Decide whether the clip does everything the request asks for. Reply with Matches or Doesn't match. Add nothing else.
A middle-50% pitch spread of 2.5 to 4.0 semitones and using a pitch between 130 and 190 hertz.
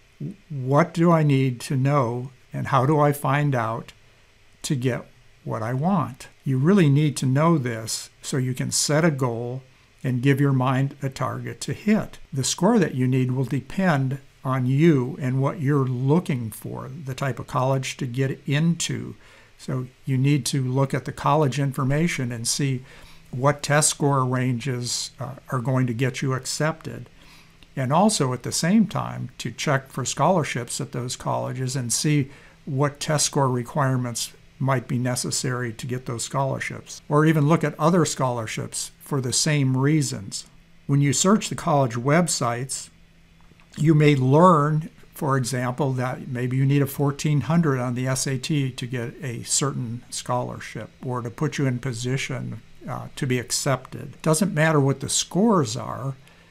Matches